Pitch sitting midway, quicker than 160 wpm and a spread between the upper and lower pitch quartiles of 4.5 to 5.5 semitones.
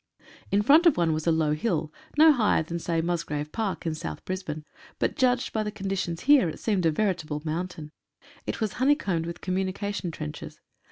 Yes: medium, 180 Hz; average, 200 wpm; average, 5.0 semitones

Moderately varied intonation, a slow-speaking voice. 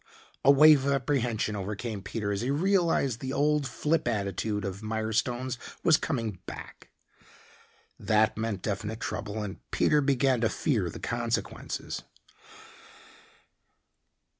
Yes: average, 4.5 semitones; slow, 120 wpm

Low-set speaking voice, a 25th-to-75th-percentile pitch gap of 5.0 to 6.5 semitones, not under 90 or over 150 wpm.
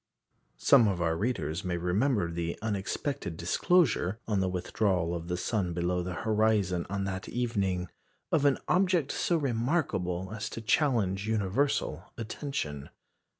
Yes: low, 100 Hz; average, 5.3 semitones; average, 140 wpm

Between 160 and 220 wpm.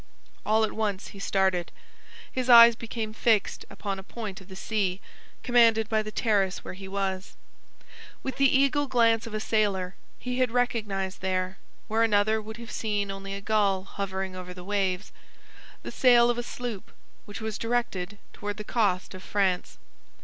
Yes: average, 170 wpm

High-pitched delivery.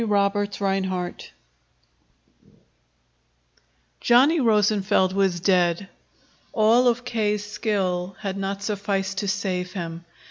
Yes: high, 200 Hz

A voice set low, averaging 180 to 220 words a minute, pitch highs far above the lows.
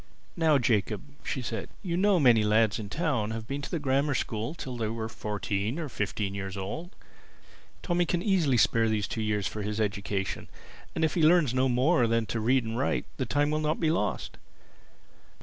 Yes: low, 120 Hz; fast, 205 wpm; wide, 6.2 semitones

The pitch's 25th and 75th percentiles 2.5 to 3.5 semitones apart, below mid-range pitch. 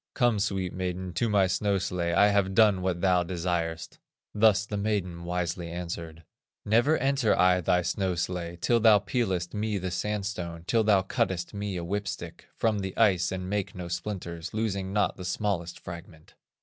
Yes: average, 3.0 semitones; very low, 95 Hz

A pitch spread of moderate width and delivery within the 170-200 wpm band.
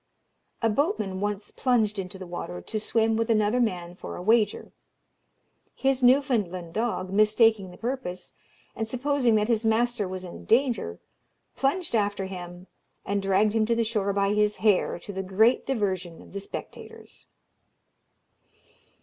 No: average, 3.6 semitones; average, 150 wpm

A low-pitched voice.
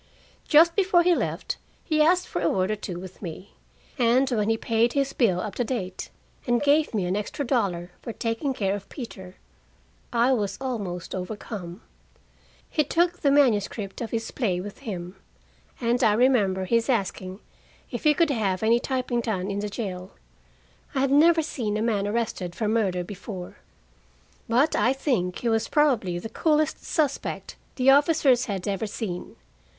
No: high, 225 Hz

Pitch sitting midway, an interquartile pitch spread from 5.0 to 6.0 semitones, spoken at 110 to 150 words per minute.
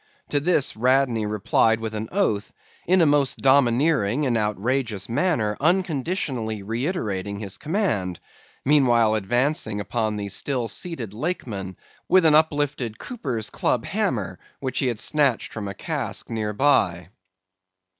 No: low, 120 Hz; wide, 5.6 semitones; slow, 135 wpm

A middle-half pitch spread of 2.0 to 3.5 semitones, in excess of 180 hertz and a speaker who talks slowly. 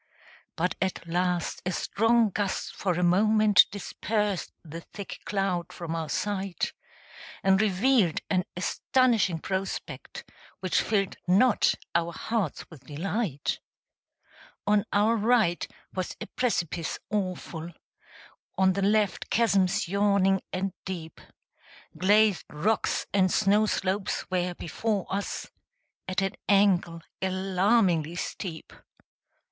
Yes: average, 2.8 semitones; high, 190 Hz; slow, 110 wpm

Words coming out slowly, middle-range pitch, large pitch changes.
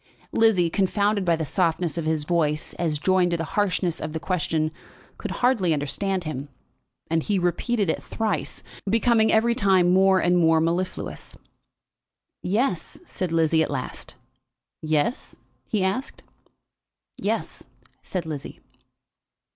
No: slow, 130 wpm; medium, 180 Hz; average, 3.8 semitones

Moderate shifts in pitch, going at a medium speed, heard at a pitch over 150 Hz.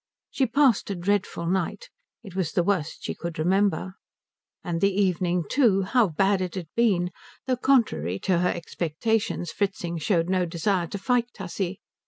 Yes: average, 3.0 semitones; average, 165 wpm; high, 190 Hz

